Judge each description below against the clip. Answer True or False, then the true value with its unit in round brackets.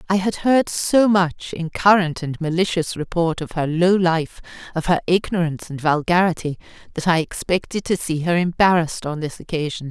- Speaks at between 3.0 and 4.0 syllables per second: False (5.1 syllables/s)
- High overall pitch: False (170 Hz)